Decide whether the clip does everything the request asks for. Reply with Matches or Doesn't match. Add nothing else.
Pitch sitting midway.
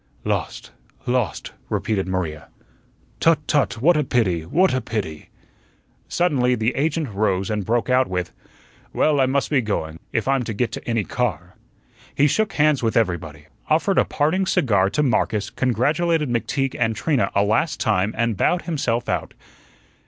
Doesn't match